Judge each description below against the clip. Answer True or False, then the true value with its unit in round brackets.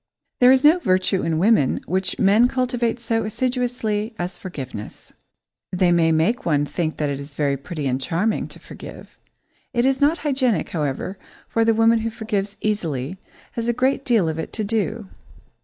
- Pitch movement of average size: False (6.4 semitones)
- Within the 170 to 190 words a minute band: True (175 wpm)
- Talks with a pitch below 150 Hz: False (210 Hz)